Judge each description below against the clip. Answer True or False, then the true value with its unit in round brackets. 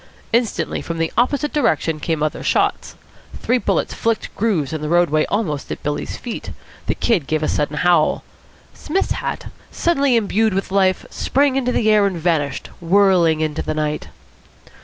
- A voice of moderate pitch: True (180 Hz)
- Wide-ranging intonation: True (6.7 semitones)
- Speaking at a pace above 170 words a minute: False (165 wpm)